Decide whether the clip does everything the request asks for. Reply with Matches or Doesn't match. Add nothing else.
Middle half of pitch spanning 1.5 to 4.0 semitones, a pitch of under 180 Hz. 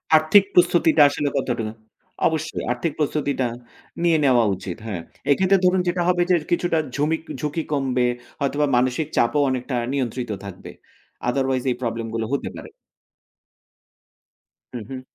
Doesn't match